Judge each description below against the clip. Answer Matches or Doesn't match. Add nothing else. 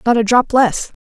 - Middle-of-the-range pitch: Doesn't match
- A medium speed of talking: Doesn't match